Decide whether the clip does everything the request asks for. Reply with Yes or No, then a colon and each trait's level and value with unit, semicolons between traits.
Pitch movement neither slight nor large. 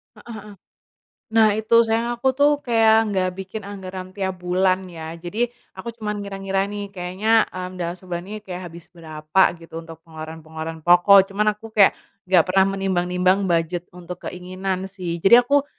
Yes: average, 3.1 semitones